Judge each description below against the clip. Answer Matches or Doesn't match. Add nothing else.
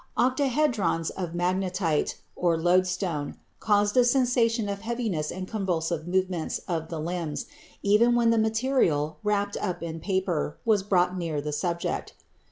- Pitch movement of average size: Matches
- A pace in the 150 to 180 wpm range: Doesn't match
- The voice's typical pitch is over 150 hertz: Matches